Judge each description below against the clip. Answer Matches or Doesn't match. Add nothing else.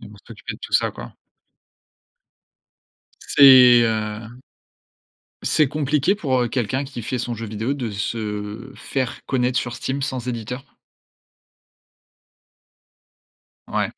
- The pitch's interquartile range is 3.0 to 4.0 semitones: Matches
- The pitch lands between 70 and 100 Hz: Doesn't match